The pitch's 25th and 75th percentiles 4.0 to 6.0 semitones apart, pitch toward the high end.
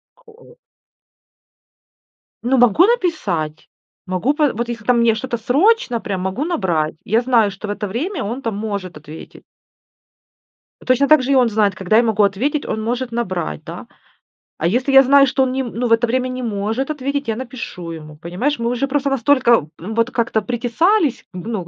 Yes: average, 4.8 semitones; high, 235 Hz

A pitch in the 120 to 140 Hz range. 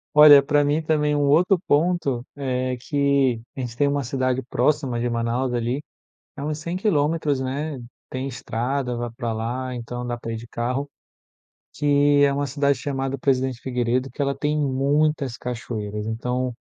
Yes: low, 135 Hz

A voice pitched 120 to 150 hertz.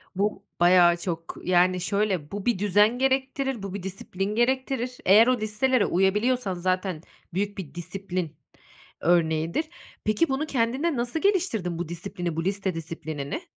No: high, 195 Hz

